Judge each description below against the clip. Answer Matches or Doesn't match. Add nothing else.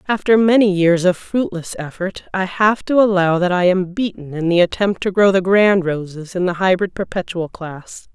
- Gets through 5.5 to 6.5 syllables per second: Doesn't match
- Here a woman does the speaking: Matches